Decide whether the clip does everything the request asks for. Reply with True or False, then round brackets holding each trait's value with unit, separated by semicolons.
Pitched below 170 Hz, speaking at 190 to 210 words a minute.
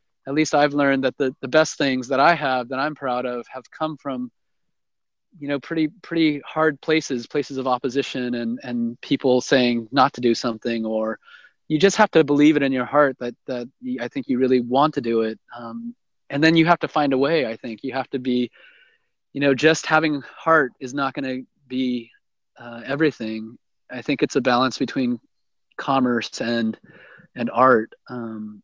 True (135 Hz; 195 wpm)